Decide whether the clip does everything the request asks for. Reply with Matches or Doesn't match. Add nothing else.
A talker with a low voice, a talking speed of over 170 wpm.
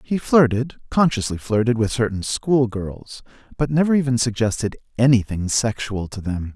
Doesn't match